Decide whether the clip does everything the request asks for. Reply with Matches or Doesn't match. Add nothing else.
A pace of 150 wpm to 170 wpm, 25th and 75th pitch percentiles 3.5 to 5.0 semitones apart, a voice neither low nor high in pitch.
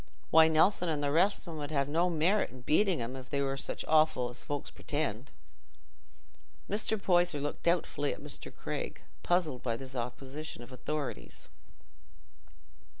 Matches